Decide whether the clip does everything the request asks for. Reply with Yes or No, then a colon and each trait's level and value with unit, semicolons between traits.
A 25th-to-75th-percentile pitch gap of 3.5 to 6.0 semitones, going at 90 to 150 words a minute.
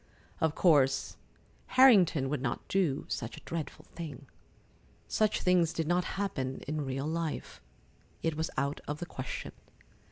Yes: average, 4.0 semitones; average, 140 wpm